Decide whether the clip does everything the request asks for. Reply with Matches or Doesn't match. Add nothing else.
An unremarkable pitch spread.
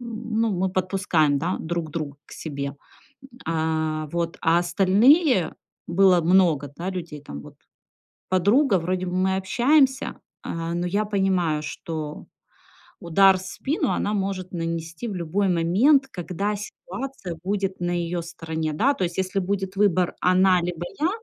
Matches